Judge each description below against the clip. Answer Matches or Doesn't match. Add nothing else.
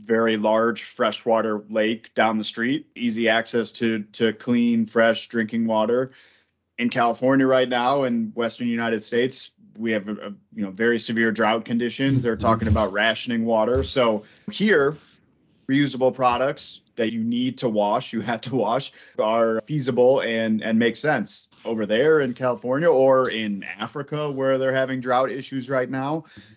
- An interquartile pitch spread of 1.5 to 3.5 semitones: Matches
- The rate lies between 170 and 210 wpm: Doesn't match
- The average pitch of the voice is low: Matches